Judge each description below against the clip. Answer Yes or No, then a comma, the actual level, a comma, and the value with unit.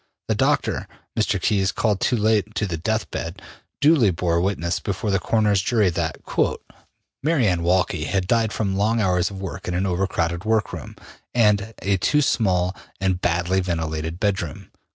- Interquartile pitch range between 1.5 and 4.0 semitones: Yes, average, 3.4 semitones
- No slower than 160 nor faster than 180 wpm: Yes, average, 170 wpm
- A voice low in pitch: Yes, very low, 95 Hz